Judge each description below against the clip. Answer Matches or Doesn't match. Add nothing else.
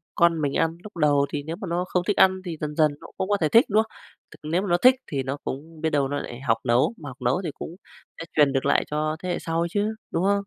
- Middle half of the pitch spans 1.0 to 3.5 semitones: Doesn't match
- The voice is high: Doesn't match